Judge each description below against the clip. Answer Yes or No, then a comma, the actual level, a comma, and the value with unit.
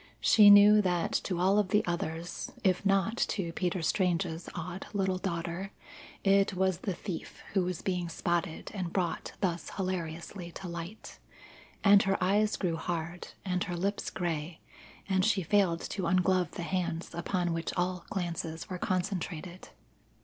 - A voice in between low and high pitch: Yes, medium, 180 Hz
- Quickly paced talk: No, average, 155 wpm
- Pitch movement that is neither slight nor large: No, narrow, 2.2 semitones